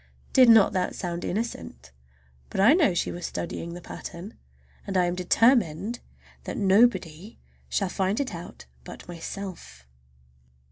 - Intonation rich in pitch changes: No, average, 4.3 semitones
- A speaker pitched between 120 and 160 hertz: No, high, 190 Hz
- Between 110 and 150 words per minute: Yes, average, 140 wpm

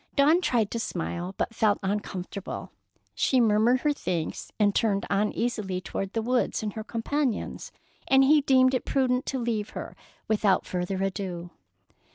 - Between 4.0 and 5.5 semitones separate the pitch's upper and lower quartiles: Yes, average, 4.6 semitones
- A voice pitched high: Yes, high, 220 Hz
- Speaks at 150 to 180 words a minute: Yes, average, 160 wpm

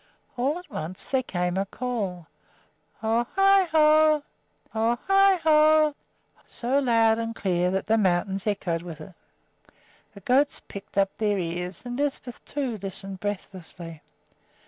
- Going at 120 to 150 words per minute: Yes, average, 140 wpm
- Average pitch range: No, wide, 7.2 semitones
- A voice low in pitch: No, high, 220 Hz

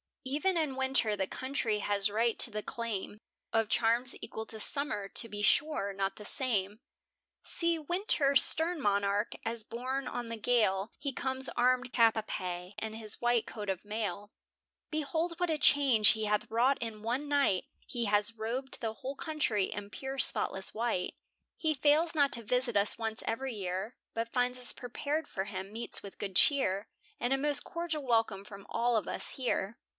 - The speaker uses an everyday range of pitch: Yes, average, 4.5 semitones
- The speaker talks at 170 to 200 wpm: Yes, average, 180 wpm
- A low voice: No, high, 230 Hz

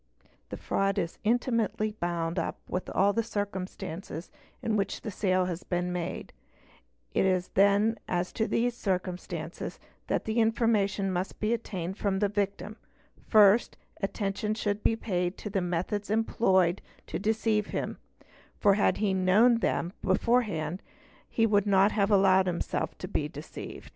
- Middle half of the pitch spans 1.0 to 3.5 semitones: Yes, average, 2.7 semitones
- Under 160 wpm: Yes, average, 150 wpm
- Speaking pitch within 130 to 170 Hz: No, high, 200 Hz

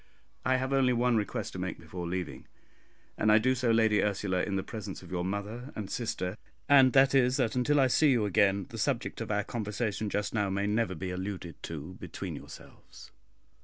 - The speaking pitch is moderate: No, low, 105 Hz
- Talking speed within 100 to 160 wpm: No, average, 200 wpm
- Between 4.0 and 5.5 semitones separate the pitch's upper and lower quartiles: Yes, average, 4.4 semitones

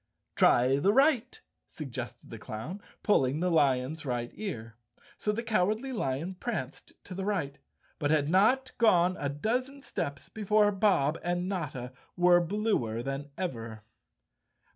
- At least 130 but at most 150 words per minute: Yes, average, 140 wpm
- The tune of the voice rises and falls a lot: Yes, wide, 7.7 semitones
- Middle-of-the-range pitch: Yes, medium, 175 Hz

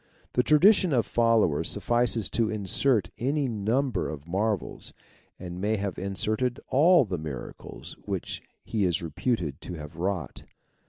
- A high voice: No, low, 105 Hz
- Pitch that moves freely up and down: Yes, wide, 5.7 semitones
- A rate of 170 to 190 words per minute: No, average, 145 wpm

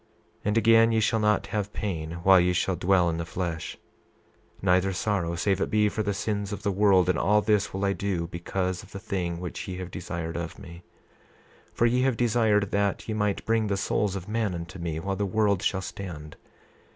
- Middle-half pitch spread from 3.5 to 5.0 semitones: No, average, 3.0 semitones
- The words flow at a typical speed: No, fast, 215 wpm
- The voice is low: Yes, very low, 95 Hz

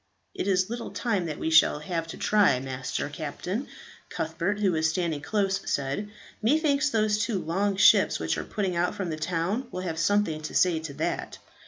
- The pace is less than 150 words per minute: No, average, 190 wpm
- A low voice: No, medium, 185 Hz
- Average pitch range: Yes, average, 4.4 semitones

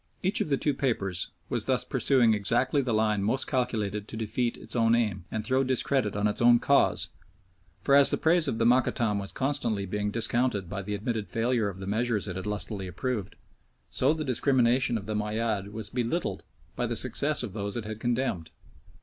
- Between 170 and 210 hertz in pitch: No, low, 115 Hz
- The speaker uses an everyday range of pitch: Yes, average, 3.7 semitones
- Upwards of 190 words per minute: Yes, average, 200 wpm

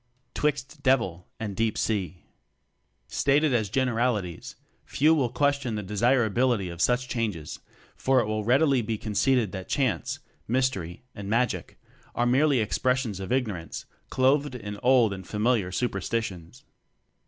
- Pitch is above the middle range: No, low, 115 Hz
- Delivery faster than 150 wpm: No, slow, 135 wpm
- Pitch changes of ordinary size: Yes, average, 4.3 semitones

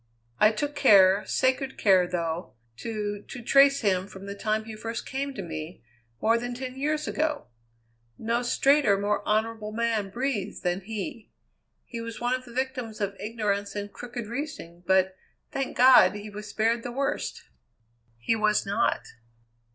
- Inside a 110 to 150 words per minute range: No, average, 160 wpm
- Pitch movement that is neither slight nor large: Yes, average, 3.9 semitones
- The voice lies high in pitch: Yes, high, 220 Hz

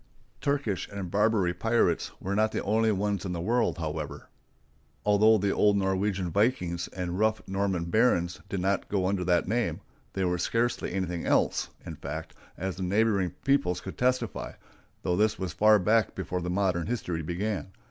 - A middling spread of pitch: Yes, average, 3.3 semitones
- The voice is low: Yes, very low, 95 Hz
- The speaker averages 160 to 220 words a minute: Yes, average, 170 wpm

